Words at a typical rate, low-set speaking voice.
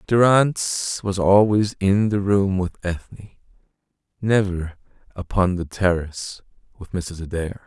No: slow, 115 wpm; very low, 95 Hz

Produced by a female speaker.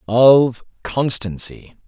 No: male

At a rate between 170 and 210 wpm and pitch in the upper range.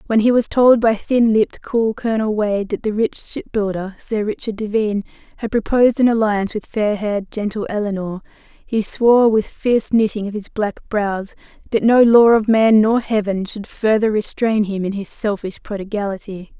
Yes: average, 180 wpm; high, 215 Hz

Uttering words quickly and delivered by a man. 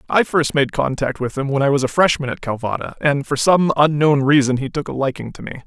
Yes: fast, 255 wpm; male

